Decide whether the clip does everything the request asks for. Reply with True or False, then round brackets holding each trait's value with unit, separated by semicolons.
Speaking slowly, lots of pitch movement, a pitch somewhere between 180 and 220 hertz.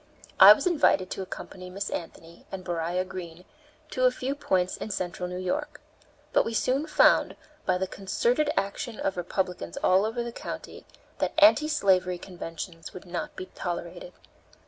False (165 wpm; 5.9 semitones; 190 Hz)